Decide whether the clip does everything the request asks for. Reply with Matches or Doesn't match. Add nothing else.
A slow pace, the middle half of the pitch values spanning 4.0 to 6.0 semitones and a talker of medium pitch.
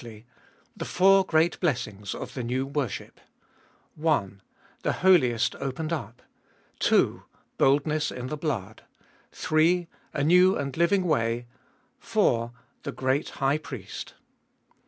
Matches